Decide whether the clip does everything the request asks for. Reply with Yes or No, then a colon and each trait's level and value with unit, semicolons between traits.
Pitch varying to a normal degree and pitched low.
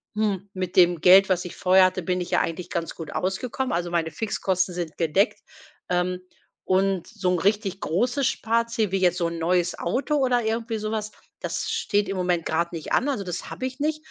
No: average, 3.8 semitones; medium, 185 Hz